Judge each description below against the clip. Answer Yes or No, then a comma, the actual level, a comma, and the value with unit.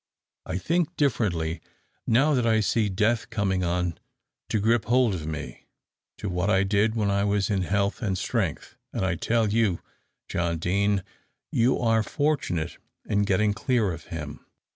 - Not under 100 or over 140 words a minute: No, average, 165 wpm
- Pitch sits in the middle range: No, low, 100 Hz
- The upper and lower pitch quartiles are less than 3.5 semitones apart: No, average, 4.0 semitones